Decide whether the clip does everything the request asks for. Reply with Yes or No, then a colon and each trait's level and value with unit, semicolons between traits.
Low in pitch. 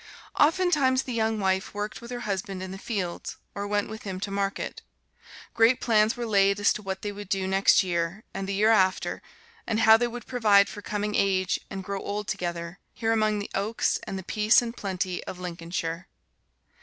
No: high, 205 Hz